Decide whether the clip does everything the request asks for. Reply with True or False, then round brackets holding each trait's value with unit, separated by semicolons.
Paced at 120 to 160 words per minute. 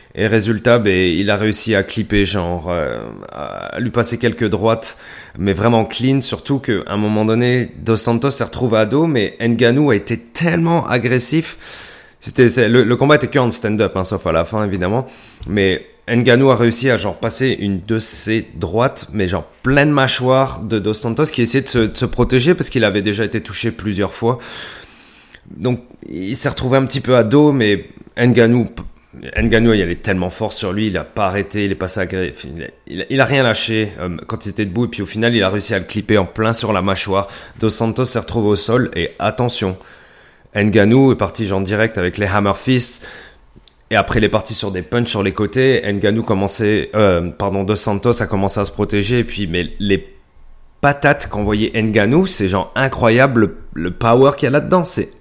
False (210 wpm)